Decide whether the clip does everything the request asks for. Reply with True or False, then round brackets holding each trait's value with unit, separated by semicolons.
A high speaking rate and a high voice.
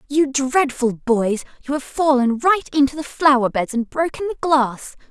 False (175 wpm; 270 Hz)